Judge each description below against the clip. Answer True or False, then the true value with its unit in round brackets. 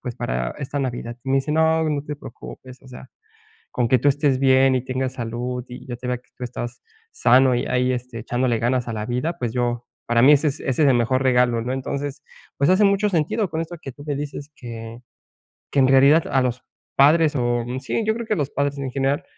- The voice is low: True (130 Hz)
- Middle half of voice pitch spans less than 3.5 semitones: True (2.9 semitones)